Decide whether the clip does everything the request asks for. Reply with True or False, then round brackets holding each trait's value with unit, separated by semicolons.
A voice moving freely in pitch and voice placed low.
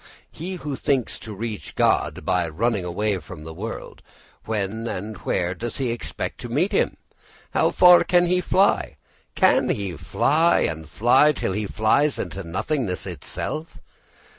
True (8.1 semitones; 110 Hz)